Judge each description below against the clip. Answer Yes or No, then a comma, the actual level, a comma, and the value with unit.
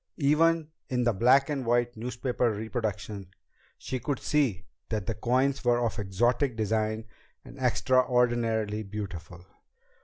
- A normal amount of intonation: Yes, average, 3.1 semitones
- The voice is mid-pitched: No, low, 120 Hz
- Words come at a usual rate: No, slow, 125 wpm